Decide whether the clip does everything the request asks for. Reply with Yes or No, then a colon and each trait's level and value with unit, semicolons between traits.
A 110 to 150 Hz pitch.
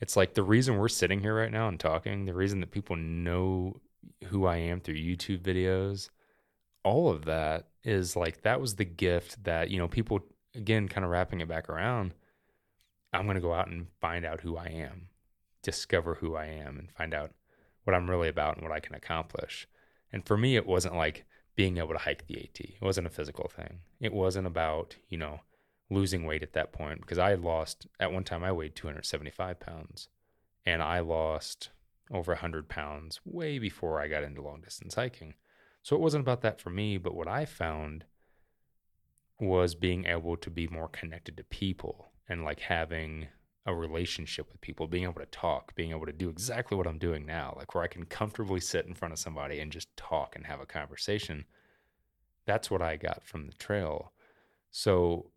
No: very low, 90 Hz